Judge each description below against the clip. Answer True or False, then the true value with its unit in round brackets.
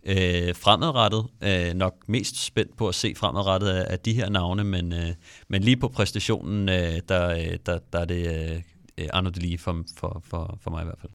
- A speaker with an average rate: True (205 wpm)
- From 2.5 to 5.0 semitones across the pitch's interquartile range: True (3.4 semitones)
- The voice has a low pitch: True (95 Hz)